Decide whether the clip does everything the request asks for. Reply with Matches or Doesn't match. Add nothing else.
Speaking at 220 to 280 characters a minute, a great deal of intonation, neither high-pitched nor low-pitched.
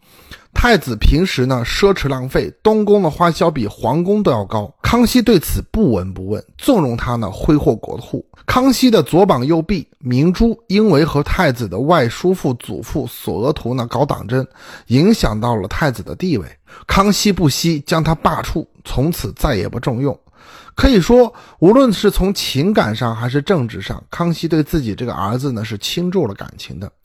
Matches